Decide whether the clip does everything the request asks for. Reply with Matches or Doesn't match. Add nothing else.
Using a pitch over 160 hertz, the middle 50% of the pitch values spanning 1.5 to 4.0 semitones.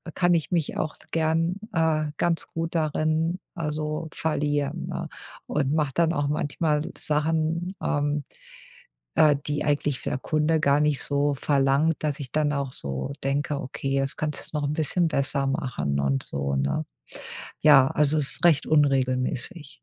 Doesn't match